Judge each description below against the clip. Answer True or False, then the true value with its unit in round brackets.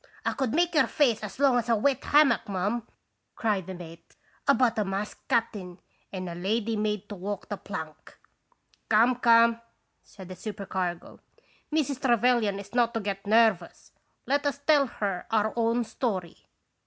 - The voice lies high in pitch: True (220 Hz)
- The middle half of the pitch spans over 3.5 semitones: True (4.0 semitones)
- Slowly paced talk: False (175 wpm)